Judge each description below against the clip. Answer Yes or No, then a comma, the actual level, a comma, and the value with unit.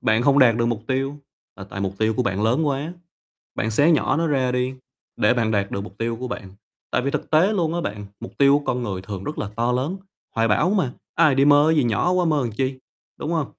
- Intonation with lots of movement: No, average, 4.9 semitones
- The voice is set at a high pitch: No, low, 125 Hz